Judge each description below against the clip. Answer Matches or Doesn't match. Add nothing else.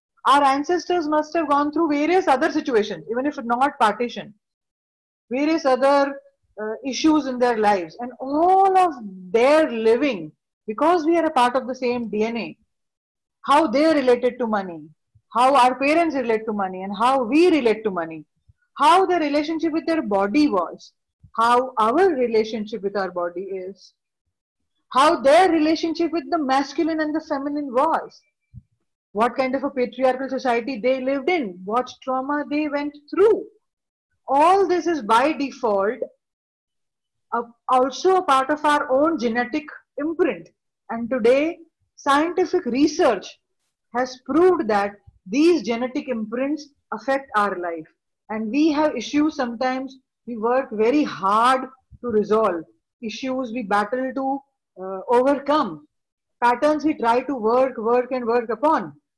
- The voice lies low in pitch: Doesn't match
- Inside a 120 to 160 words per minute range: Matches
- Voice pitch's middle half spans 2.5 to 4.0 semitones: Doesn't match